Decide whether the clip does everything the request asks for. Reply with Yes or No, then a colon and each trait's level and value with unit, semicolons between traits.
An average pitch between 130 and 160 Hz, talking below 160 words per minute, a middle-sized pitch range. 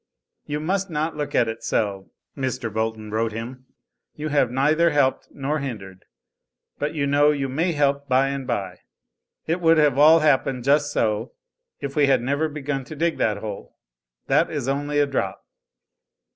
No: medium, 140 Hz; average, 170 wpm; average, 4.1 semitones